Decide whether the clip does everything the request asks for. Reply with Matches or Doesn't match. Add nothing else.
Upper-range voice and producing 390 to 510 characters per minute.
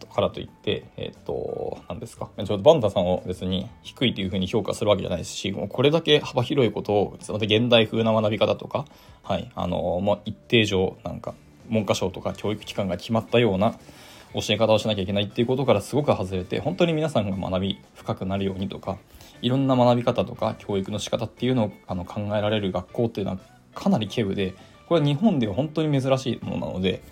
Doesn't match